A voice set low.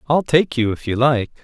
Yes: low, 130 Hz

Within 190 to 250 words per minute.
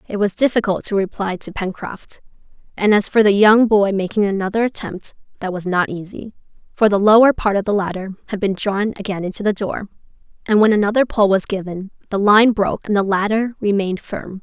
Yes: average, 200 wpm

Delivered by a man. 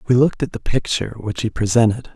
Yes: male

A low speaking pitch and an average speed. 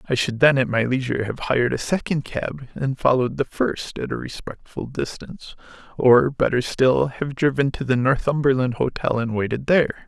Yes: low, 130 Hz; average, 185 wpm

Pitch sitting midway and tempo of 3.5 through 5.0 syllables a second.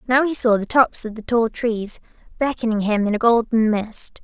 No: high, 230 Hz; 4.9 syllables/s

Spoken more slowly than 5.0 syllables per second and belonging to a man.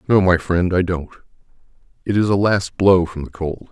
No: 5.1 syllables/s; male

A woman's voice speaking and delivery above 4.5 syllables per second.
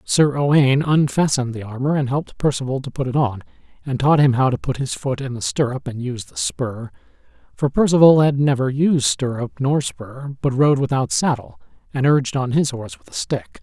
No: male; 5.4 syllables/s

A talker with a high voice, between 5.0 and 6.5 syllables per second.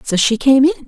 Yes: very high, 260 Hz; 6.2 syllables/s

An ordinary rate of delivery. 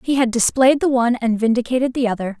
No: fast, 225 wpm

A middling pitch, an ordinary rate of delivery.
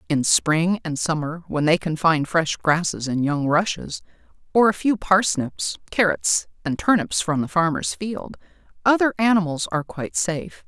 Yes: medium, 160 Hz; average, 165 wpm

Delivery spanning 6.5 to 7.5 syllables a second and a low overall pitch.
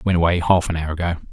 Yes: 7.0 syllables/s; very low, 85 Hz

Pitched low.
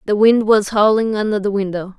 No: high, 210 Hz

